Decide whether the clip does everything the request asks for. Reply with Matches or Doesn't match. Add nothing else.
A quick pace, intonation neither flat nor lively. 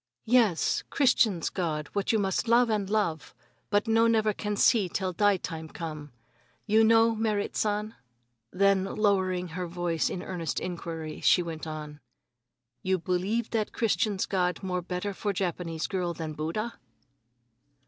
Doesn't match